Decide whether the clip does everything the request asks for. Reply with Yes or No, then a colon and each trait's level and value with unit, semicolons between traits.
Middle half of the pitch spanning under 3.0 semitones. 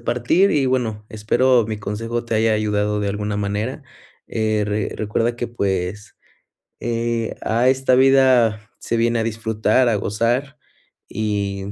Yes: narrow, 2.5 semitones